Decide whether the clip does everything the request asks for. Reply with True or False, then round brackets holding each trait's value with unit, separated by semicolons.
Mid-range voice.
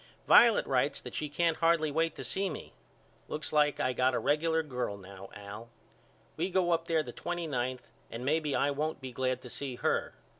True (145 Hz)